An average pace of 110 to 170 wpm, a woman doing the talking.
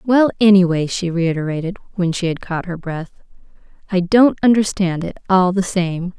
Yes: average, 165 wpm; female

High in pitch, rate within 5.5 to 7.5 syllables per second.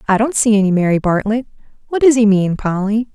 Yes: high, 215 Hz; 6.0 syllables/s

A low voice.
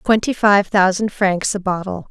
No: high, 195 Hz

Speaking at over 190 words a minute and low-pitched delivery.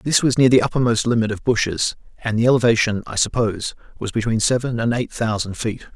Yes: average, 200 wpm; low, 115 Hz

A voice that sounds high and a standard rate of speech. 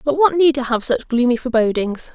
No: very high, 265 Hz; fast, 225 wpm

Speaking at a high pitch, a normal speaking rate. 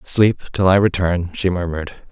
No: very low, 90 Hz; average, 170 wpm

